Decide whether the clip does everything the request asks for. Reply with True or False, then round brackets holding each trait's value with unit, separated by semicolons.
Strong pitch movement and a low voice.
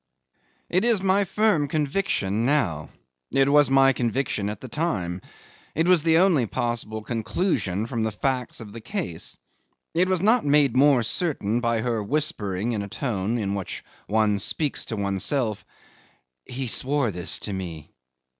True (6.2 semitones; 120 Hz)